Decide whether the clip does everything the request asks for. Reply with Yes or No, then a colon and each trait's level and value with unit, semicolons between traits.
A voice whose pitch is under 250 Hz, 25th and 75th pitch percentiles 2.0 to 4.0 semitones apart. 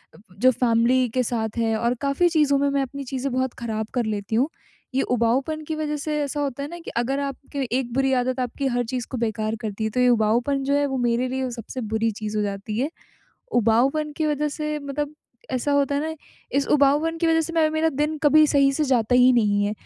No: very high, 265 Hz; average, 3.7 semitones